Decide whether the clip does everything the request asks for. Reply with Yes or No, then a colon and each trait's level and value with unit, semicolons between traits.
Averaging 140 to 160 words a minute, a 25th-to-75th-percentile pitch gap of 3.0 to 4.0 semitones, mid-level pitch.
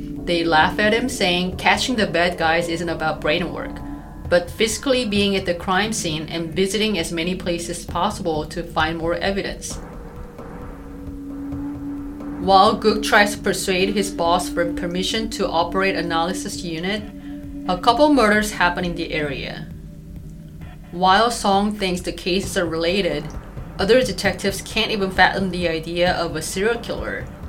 Yes: average, 150 wpm; average, 3.6 semitones; medium, 180 Hz